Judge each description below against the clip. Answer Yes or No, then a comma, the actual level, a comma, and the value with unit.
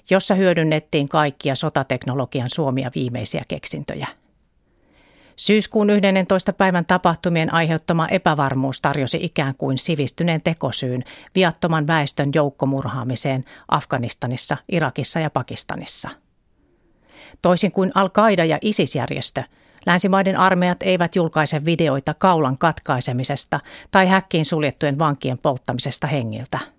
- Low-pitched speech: No, medium, 155 Hz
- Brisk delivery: No, slow, 95 wpm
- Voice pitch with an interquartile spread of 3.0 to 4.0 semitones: No, average, 4.7 semitones